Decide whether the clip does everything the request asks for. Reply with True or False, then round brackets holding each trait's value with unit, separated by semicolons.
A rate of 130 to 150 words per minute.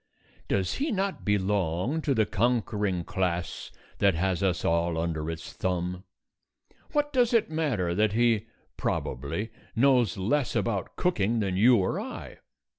True (140 wpm)